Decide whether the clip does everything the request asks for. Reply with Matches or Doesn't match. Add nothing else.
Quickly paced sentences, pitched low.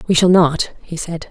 Doesn't match